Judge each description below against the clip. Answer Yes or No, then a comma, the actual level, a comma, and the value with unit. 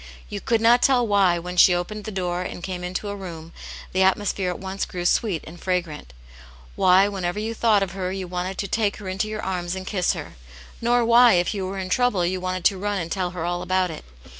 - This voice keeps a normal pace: No, fast, 240 wpm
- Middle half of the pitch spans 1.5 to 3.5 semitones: Yes, narrow, 2.5 semitones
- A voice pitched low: No, medium, 185 Hz